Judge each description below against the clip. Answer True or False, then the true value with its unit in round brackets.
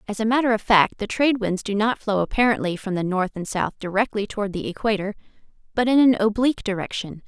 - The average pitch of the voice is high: True (210 Hz)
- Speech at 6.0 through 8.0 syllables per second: True (6.3 syllables/s)